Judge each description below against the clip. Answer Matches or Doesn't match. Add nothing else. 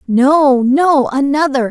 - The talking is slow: Matches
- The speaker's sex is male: Doesn't match